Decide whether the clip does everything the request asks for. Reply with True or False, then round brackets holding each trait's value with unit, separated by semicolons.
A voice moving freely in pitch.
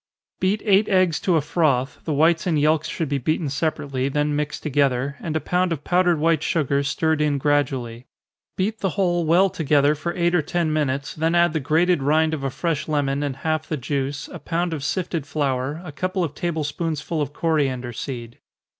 False (3.2 semitones)